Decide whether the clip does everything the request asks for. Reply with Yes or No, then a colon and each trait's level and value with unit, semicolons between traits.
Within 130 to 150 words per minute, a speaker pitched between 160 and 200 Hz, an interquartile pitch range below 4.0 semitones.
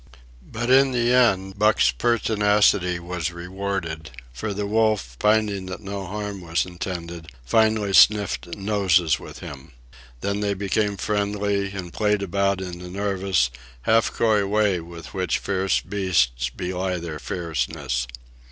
No: slow, 135 wpm; very low, 95 Hz; average, 3.2 semitones